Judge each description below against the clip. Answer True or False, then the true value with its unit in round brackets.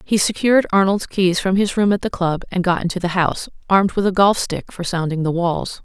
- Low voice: False (185 Hz)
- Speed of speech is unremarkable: False (245 wpm)